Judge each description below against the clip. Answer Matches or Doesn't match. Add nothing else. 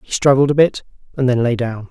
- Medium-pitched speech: Doesn't match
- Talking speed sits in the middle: Doesn't match